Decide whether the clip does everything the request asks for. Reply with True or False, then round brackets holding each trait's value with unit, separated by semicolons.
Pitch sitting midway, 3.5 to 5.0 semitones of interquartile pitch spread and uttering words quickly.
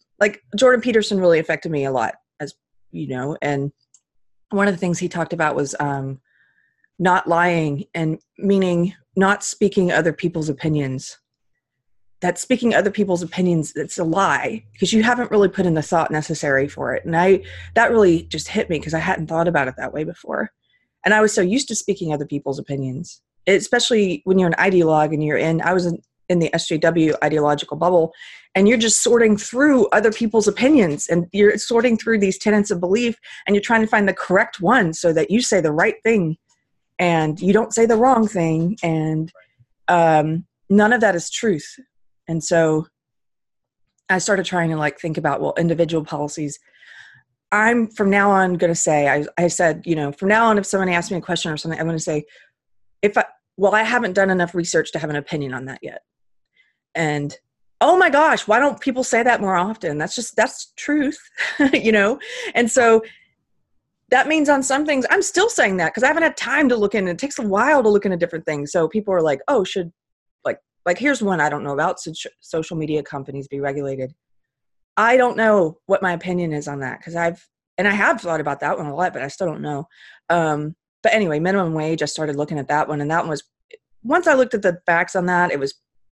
False (175 Hz; 5.6 semitones; 215 wpm)